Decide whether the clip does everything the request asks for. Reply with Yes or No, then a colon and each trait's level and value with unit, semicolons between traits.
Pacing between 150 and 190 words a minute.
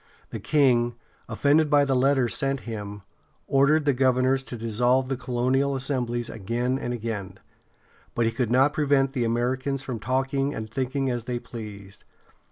Yes: average, 160 wpm